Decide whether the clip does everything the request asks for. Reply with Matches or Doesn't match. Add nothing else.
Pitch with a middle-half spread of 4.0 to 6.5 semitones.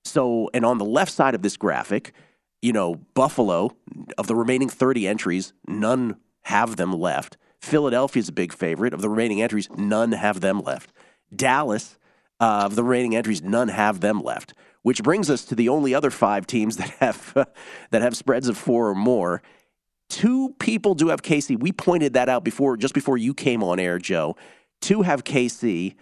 Matches